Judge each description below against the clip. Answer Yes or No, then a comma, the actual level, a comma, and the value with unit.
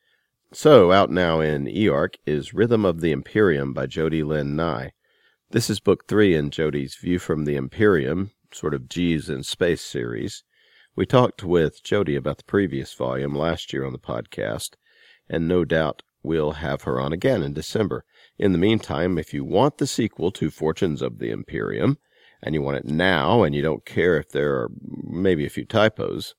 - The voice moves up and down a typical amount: Yes, average, 3.3 semitones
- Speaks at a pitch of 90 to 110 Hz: No, very low, 75 Hz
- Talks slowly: No, average, 185 wpm